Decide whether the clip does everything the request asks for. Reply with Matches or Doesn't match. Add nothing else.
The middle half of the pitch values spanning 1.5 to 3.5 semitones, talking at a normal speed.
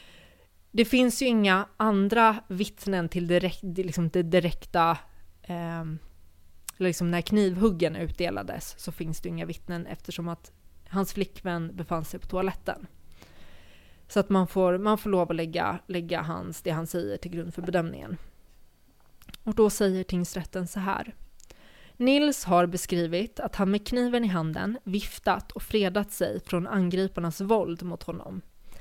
Matches